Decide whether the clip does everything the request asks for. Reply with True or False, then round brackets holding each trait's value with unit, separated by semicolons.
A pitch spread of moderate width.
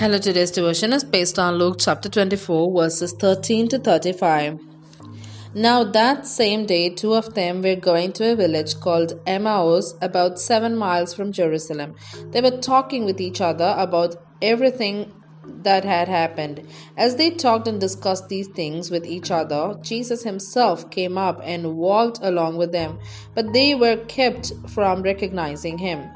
True (4.5 semitones)